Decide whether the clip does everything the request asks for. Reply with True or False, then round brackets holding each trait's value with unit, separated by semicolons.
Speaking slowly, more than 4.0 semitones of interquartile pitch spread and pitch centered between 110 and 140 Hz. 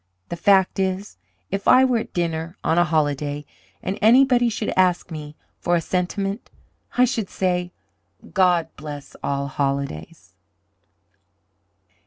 False (130 wpm; 4.5 semitones; 180 Hz)